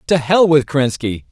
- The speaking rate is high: No, average, 180 wpm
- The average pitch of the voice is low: No, medium, 145 Hz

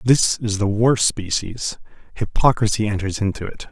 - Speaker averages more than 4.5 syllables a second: Yes, 4.7 syllables/s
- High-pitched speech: No, low, 105 Hz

